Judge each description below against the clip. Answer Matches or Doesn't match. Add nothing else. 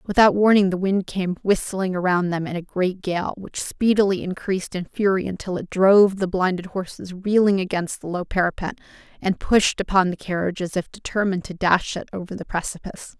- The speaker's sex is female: Matches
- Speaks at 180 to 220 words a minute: Matches